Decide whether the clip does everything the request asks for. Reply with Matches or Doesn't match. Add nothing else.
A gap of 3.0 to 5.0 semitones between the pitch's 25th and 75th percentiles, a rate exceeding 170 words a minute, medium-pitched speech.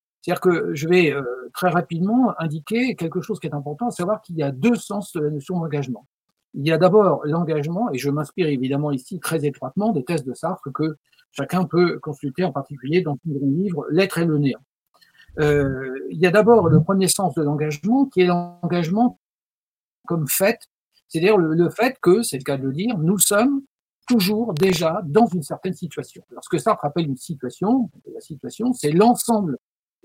Doesn't match